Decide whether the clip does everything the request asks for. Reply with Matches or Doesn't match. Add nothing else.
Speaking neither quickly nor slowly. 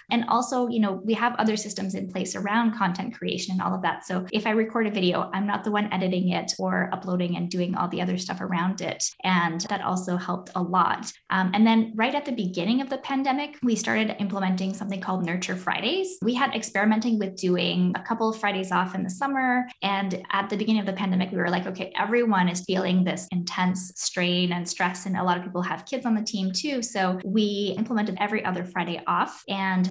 Doesn't match